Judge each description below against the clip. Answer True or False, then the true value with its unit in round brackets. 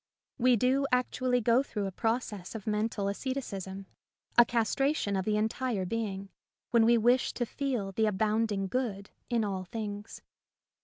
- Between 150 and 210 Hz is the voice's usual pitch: False (220 Hz)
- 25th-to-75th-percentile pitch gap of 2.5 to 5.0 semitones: True (3.6 semitones)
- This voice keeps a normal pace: True (150 wpm)